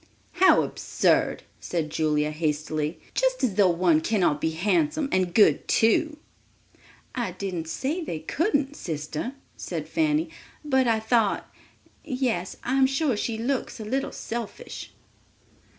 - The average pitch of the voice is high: Yes, high, 220 Hz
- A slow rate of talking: Yes, slow, 125 wpm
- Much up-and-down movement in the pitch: Yes, wide, 8.3 semitones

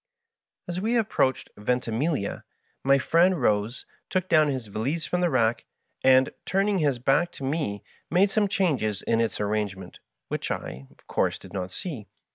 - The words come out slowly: No, average, 160 wpm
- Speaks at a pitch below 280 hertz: Yes, low, 135 Hz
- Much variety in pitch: Yes, wide, 8.3 semitones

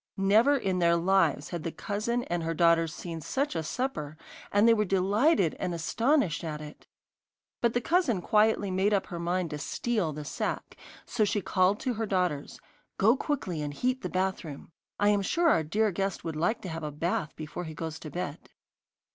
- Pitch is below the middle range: No, medium, 185 Hz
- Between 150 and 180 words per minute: No, average, 195 wpm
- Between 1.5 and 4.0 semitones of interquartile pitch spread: No, average, 5.0 semitones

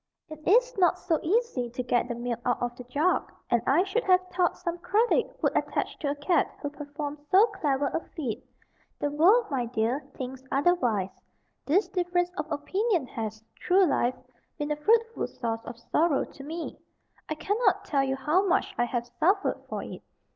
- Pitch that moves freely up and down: Yes, wide, 6.4 semitones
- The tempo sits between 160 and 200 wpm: Yes, average, 185 wpm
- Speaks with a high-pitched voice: Yes, very high, 300 Hz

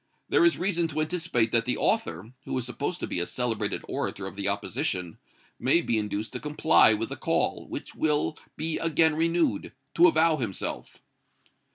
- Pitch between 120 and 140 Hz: Yes, low, 135 Hz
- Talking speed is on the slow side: No, average, 180 wpm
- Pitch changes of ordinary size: No, wide, 7.1 semitones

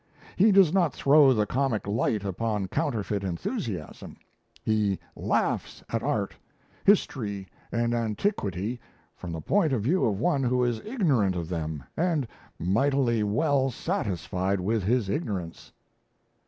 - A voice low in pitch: Yes, low, 115 Hz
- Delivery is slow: Yes, slow, 130 wpm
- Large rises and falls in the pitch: Yes, wide, 6.2 semitones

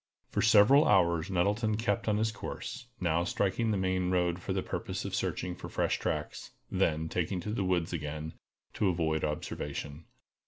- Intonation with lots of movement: No, average, 4.1 semitones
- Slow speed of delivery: No, average, 170 wpm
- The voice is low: Yes, very low, 90 Hz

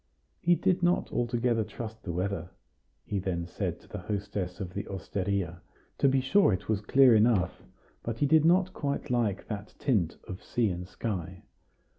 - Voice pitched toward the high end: No, low, 105 Hz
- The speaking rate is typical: Yes, average, 175 wpm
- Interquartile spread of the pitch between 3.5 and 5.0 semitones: No, wide, 5.5 semitones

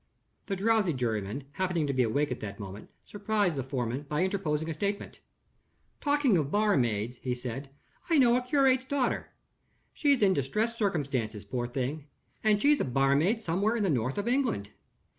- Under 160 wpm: No, average, 170 wpm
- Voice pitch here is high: No, medium, 160 Hz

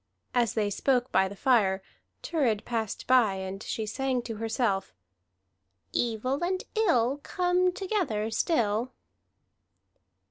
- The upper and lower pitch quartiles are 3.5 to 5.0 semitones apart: Yes, average, 4.7 semitones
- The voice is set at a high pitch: Yes, high, 235 Hz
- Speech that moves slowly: Yes, slow, 115 wpm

